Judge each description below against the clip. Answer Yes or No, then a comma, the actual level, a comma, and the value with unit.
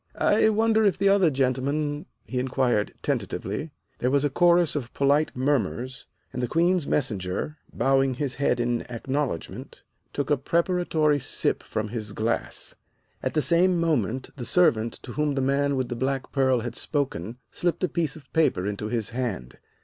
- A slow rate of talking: No, average, 170 wpm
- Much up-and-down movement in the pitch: No, average, 4.3 semitones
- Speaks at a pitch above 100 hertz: Yes, low, 135 Hz